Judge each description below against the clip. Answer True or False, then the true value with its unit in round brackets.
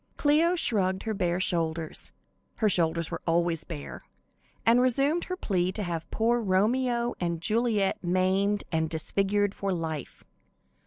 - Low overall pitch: False (190 Hz)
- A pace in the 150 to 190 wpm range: False (140 wpm)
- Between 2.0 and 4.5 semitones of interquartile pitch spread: False (5.2 semitones)